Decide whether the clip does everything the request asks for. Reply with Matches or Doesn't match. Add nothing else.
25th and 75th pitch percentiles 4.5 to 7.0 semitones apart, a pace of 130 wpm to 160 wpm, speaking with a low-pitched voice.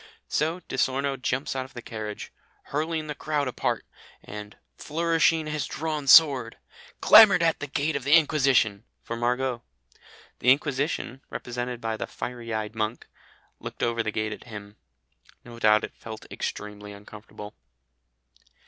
Matches